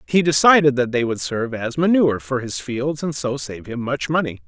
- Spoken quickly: Yes, fast, 230 wpm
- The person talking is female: No, male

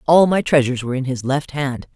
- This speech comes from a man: No, female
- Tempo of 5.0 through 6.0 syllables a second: No, 6.2 syllables/s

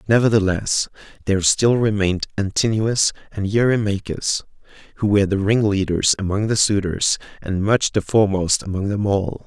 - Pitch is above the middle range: No, low, 100 Hz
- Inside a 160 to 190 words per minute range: No, slow, 135 wpm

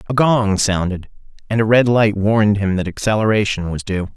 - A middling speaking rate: Yes, average, 190 wpm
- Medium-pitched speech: No, low, 105 Hz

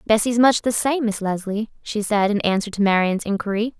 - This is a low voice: No, high, 215 Hz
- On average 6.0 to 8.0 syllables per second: No, 5.4 syllables/s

